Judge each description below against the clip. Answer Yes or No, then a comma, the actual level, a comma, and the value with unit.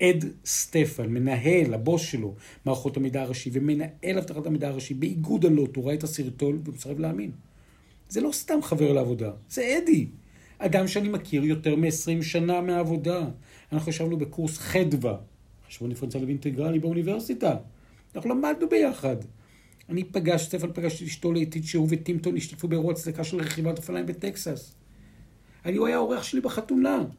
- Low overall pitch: No, medium, 160 Hz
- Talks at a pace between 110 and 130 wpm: No, fast, 150 wpm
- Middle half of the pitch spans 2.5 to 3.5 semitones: No, average, 4.5 semitones